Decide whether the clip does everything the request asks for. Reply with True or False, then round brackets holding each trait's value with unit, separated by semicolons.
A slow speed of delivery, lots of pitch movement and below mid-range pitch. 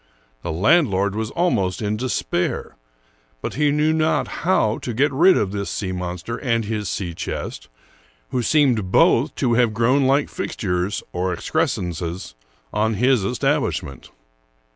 False (150 wpm; 6.4 semitones; 110 Hz)